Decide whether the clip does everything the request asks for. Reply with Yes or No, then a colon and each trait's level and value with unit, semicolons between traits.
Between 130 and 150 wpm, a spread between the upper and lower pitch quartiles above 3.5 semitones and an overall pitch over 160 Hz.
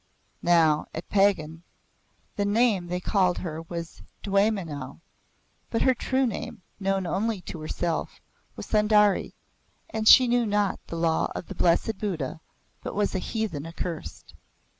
Yes: average, 140 wpm; average, 4.1 semitones; high, 190 Hz